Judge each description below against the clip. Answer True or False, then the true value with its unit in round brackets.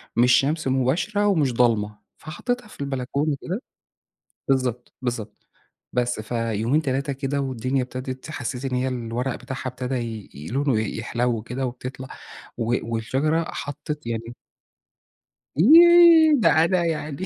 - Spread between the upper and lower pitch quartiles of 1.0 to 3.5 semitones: False (4.0 semitones)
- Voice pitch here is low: True (130 Hz)